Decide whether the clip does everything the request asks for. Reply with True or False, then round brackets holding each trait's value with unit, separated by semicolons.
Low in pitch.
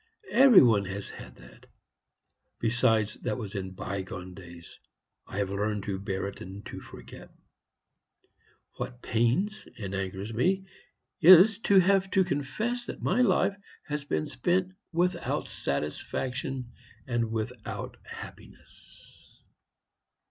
True (115 Hz)